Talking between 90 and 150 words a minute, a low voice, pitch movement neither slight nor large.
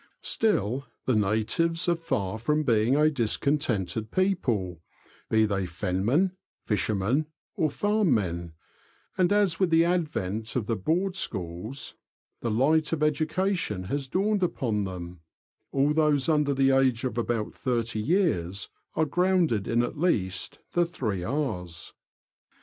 No: average, 140 wpm; low, 130 Hz; wide, 7.6 semitones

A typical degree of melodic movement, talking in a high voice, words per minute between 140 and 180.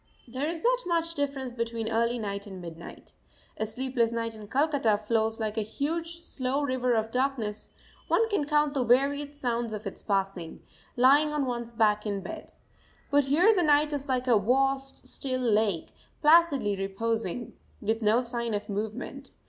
Yes: average, 4.6 semitones; high, 245 Hz; average, 170 wpm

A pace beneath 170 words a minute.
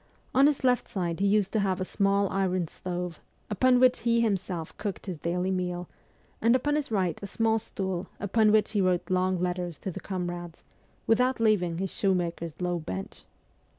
No: average, 185 wpm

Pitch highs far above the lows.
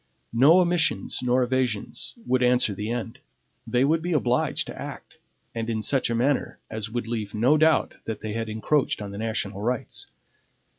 No: average, 3.2 semitones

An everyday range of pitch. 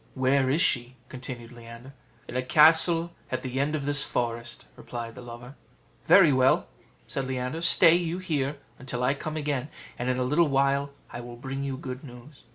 Yes: average, 3.1 semitones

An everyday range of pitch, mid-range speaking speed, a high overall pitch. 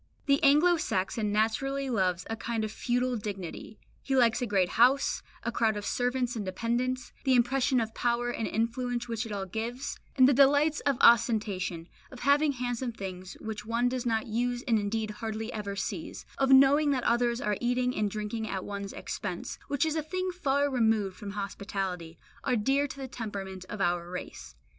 Yes: average, 3.7 semitones; average, 185 wpm; high, 235 Hz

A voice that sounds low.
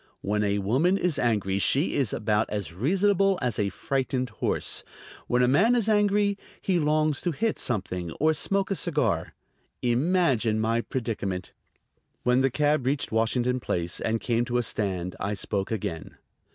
Yes: low, 125 Hz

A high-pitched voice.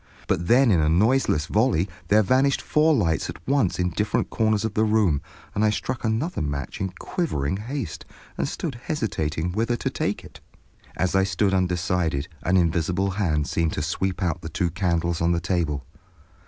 No: very low, 95 Hz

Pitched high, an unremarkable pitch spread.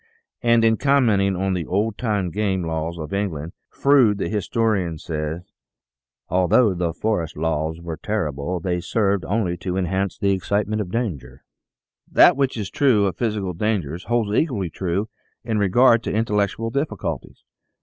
No: low, 100 Hz; average, 4.5 semitones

